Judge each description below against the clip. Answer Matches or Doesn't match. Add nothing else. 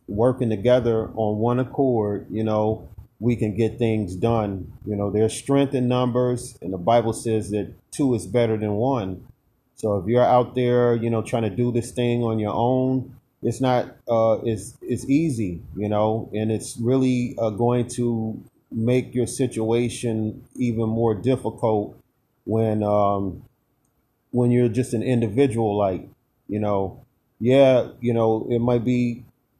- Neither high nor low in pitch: Doesn't match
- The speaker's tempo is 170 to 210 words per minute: Doesn't match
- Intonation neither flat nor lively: Doesn't match